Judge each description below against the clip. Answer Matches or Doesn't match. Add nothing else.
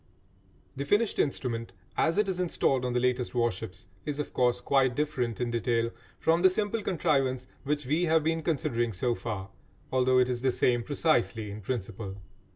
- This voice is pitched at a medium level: Doesn't match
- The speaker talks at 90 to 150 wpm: Doesn't match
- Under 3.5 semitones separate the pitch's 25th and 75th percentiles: Doesn't match